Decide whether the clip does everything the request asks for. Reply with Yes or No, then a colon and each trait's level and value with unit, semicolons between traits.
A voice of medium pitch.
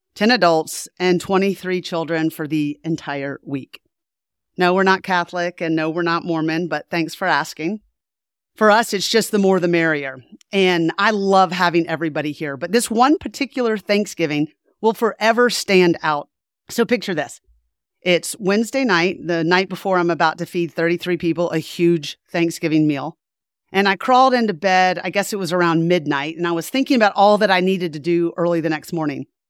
Yes: medium, 175 Hz